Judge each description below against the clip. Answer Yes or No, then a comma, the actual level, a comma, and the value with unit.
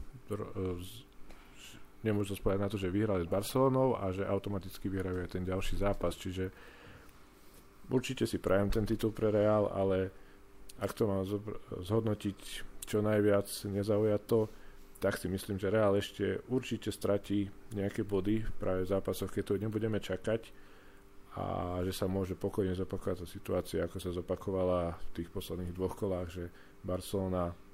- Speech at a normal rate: Yes, average, 145 wpm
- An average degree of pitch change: No, narrow, 1.9 semitones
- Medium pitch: No, low, 100 Hz